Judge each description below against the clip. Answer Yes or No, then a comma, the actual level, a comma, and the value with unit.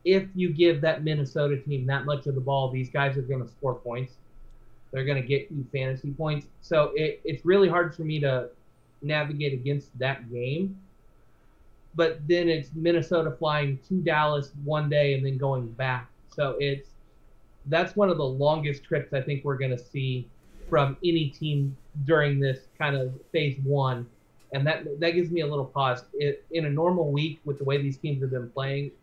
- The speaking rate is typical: Yes, average, 195 wpm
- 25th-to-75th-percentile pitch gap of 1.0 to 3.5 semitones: Yes, average, 2.8 semitones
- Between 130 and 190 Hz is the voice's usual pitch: Yes, medium, 140 Hz